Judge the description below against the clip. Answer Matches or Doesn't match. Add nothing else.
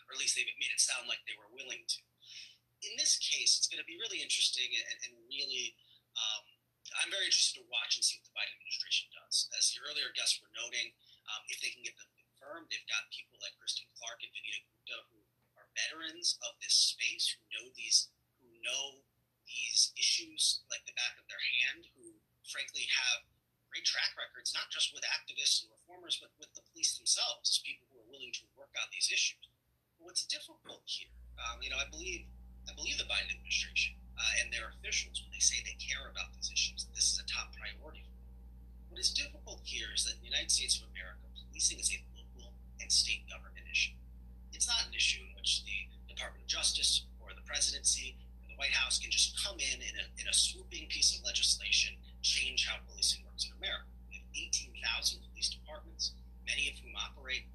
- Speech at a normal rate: Doesn't match